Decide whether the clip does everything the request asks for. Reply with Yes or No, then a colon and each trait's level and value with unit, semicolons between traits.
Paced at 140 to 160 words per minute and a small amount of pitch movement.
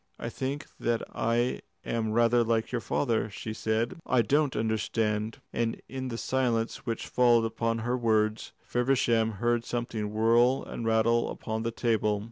Yes: average, 155 wpm; narrow, 1.4 semitones